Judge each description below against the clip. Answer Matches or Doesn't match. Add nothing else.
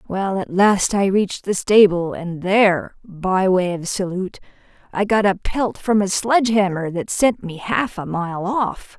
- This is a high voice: Matches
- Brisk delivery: Doesn't match